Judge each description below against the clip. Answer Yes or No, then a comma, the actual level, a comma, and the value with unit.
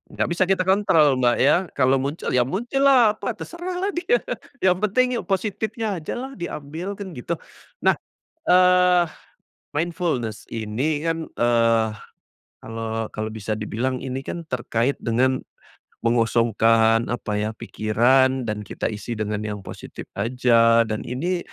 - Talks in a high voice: No, low, 130 Hz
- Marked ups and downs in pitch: Yes, wide, 8.0 semitones